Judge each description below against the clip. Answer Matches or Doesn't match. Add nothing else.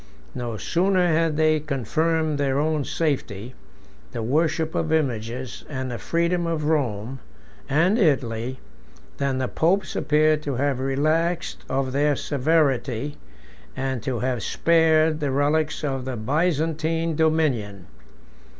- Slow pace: Matches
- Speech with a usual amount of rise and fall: Matches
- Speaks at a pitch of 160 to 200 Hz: Doesn't match